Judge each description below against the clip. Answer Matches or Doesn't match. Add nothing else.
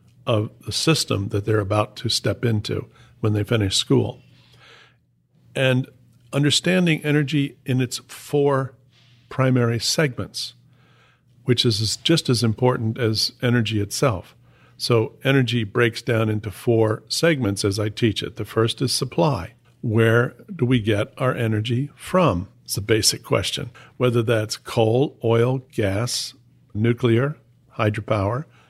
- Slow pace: Matches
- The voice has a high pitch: Doesn't match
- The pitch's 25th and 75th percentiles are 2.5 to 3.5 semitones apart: Matches